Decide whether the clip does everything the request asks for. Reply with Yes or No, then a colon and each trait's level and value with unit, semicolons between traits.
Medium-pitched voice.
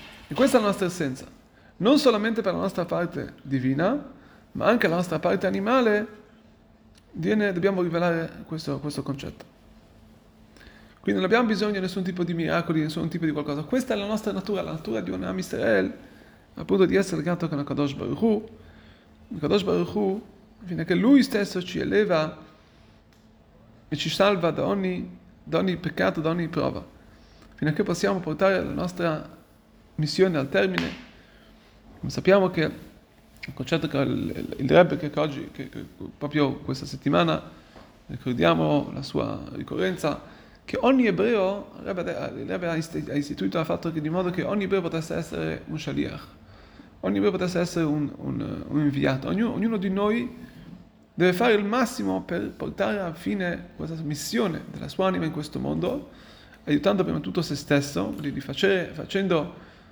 Yes: medium, 170 Hz